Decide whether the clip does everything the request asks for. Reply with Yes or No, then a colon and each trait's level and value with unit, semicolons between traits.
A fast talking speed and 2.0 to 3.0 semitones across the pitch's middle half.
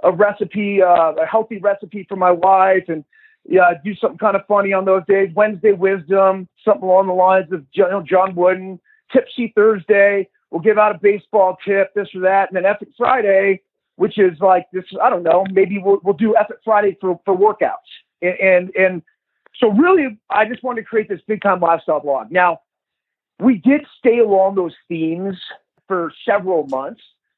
No: average, 185 wpm; narrow, 2.4 semitones